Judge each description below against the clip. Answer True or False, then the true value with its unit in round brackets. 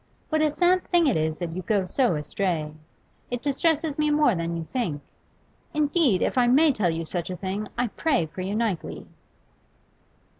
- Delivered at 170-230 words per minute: True (190 wpm)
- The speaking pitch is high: True (215 Hz)